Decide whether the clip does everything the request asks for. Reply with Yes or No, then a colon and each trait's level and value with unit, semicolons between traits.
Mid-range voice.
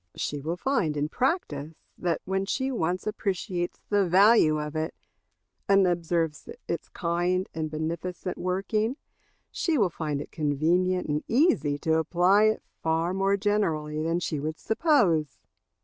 Yes: medium, 175 Hz